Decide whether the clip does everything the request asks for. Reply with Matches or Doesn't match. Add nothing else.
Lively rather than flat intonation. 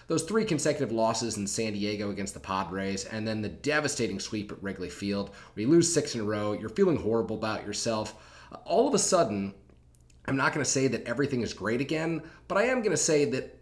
Matches